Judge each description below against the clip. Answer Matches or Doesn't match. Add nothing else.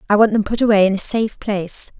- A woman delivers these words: Matches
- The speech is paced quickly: Matches